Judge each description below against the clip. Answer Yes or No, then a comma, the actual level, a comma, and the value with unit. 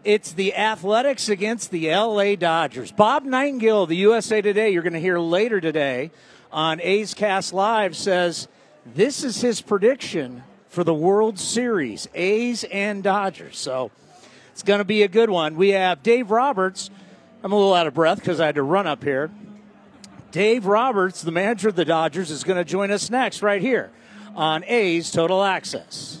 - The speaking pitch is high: Yes, high, 195 Hz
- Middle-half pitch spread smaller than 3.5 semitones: No, average, 3.9 semitones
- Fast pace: No, average, 180 wpm